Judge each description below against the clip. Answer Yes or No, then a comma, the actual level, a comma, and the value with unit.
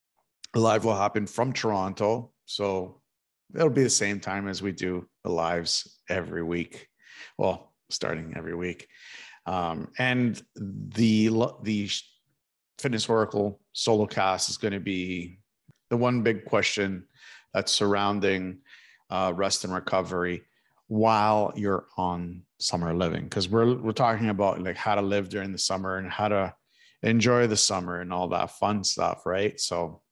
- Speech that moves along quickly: No, average, 145 wpm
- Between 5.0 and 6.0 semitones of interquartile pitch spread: No, average, 3.2 semitones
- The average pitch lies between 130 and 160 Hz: No, low, 100 Hz